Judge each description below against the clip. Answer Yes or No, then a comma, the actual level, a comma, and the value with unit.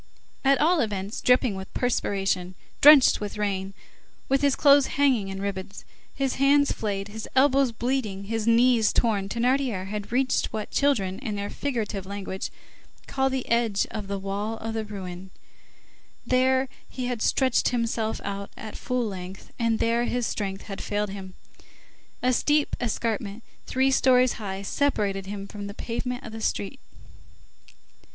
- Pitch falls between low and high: No, high, 220 Hz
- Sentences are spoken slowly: No, average, 155 wpm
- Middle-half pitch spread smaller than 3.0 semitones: No, average, 4.4 semitones